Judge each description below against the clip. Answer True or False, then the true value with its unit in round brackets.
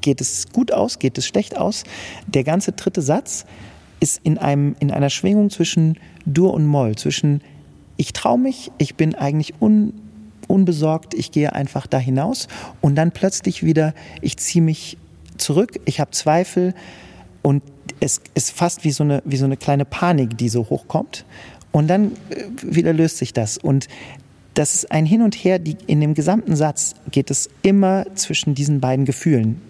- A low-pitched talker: False (155 Hz)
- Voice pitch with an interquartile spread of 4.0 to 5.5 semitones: True (4.5 semitones)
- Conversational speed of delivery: True (175 wpm)